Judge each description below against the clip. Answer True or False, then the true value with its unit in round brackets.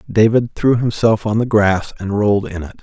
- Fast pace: True (210 wpm)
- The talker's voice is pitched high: False (105 Hz)